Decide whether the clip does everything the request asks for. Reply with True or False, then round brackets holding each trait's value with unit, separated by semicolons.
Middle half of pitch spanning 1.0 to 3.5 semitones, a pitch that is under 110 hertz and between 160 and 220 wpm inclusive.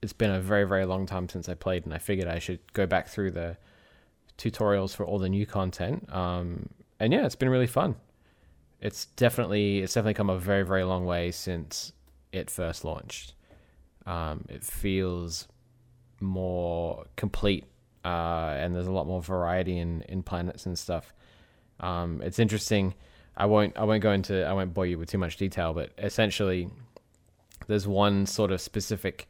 True (2.9 semitones; 95 Hz; 180 wpm)